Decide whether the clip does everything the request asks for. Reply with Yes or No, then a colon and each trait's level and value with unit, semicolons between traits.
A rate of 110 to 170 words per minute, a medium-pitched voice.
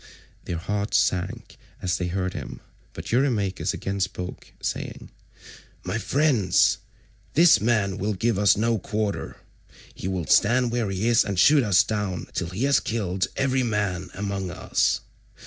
No: average, 150 wpm; low, 100 Hz